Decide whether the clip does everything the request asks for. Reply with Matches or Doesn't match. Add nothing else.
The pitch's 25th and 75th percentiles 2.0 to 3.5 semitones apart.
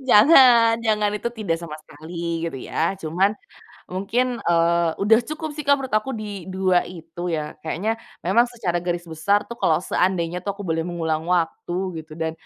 Doesn't match